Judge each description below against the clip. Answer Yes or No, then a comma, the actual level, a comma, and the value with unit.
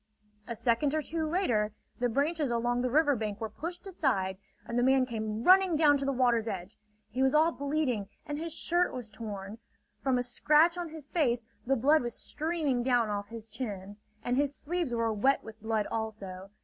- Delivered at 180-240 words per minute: Yes, average, 200 wpm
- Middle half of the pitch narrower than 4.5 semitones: No, wide, 5.4 semitones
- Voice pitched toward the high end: Yes, high, 245 Hz